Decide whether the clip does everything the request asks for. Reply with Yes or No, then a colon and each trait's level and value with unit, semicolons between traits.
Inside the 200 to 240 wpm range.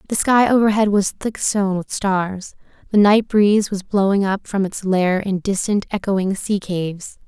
No: average, 180 wpm